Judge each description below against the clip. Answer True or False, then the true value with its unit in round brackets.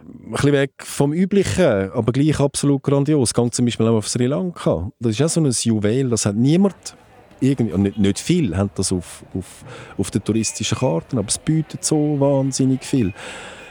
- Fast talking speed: False (190 wpm)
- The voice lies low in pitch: True (130 Hz)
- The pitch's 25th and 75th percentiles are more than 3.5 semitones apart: True (4.7 semitones)